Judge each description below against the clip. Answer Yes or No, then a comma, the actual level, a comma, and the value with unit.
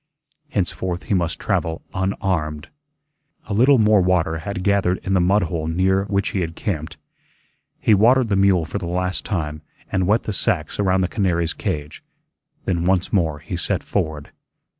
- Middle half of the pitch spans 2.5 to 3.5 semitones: Yes, average, 3.1 semitones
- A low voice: Yes, very low, 90 Hz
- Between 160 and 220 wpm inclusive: Yes, average, 170 wpm